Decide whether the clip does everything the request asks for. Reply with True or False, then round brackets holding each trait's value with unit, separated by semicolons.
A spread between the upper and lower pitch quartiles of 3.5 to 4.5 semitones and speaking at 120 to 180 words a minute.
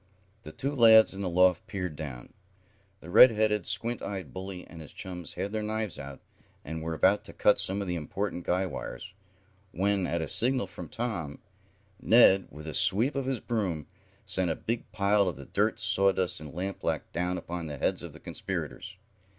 False (4.0 semitones; 190 wpm)